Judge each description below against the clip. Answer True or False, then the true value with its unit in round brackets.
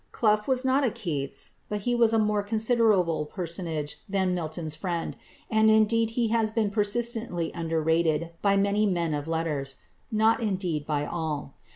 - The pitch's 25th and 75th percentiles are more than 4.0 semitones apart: True (5.2 semitones)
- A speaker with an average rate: True (160 wpm)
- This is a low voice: False (195 Hz)